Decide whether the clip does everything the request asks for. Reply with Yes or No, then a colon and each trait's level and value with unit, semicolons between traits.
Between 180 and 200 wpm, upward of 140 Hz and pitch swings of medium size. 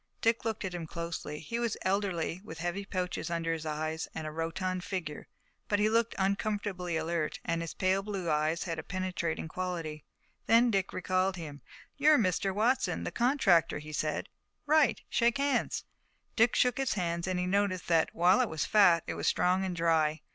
Yes: average, 185 wpm; medium, 185 Hz; average, 3.7 semitones